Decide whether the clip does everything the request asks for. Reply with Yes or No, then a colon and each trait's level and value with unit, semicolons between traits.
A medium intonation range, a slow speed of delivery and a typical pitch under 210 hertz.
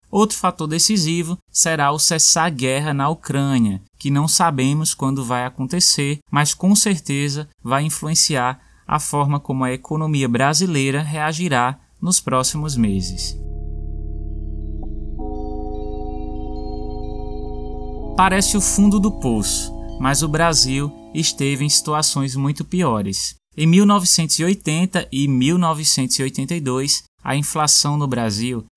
No: wide, 6.5 semitones; slow, 110 wpm; medium, 140 Hz